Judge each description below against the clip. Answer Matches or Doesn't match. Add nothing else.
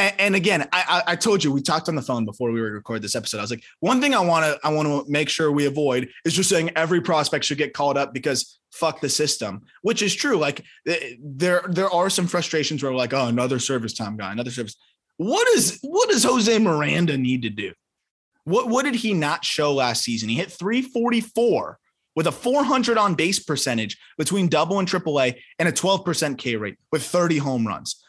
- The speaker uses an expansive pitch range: Matches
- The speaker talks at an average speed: Doesn't match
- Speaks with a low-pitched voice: Doesn't match